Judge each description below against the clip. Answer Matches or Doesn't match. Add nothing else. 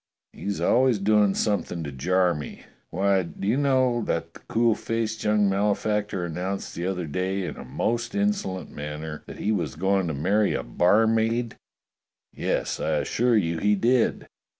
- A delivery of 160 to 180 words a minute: Matches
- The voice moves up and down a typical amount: Matches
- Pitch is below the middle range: Matches